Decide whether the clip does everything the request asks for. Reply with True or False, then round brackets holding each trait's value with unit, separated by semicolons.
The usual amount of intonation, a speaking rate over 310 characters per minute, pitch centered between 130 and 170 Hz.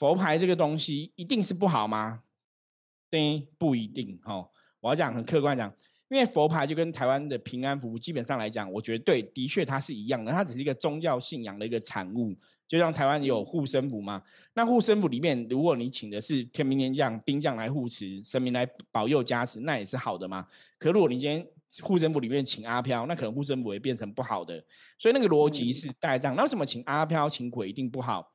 True (4.7 semitones; 330 characters per minute; 135 Hz)